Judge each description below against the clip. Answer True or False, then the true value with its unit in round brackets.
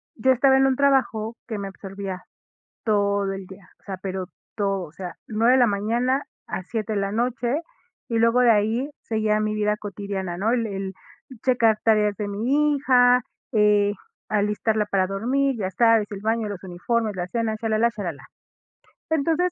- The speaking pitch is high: True (215 Hz)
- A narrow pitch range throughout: False (3.2 semitones)